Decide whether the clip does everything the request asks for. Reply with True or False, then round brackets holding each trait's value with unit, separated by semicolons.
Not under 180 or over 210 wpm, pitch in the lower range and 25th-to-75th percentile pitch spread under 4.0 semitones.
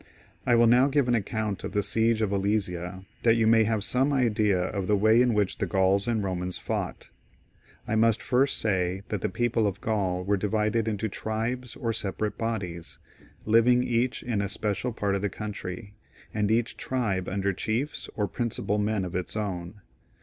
True (185 wpm; 105 Hz; 2.8 semitones)